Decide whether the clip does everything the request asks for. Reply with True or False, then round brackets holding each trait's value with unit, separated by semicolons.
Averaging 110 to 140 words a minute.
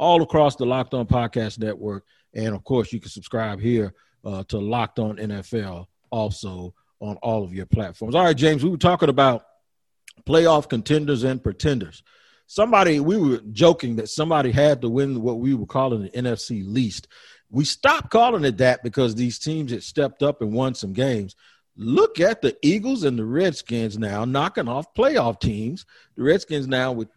False (185 wpm)